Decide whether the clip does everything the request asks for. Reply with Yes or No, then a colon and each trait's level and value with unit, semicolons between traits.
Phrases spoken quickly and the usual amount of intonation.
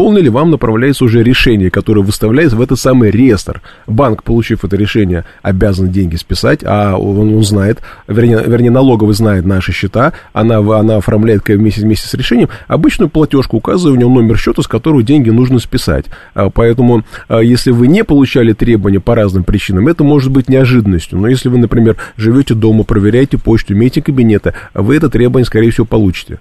Yes: fast, 175 wpm; average, 3.8 semitones